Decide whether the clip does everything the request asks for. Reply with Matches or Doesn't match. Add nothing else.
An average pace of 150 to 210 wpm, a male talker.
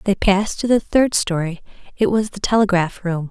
Doesn't match